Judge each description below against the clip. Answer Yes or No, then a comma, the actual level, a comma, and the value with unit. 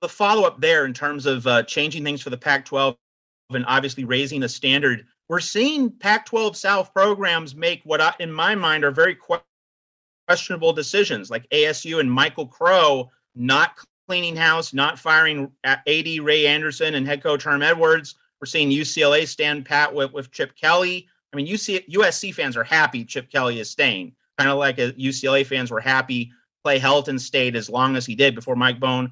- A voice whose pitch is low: No, medium, 145 Hz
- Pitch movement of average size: Yes, average, 4.2 semitones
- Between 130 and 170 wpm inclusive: No, average, 190 wpm